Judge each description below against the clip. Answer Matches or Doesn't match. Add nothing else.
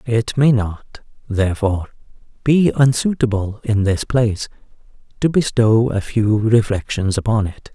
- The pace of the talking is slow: Matches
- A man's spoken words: Matches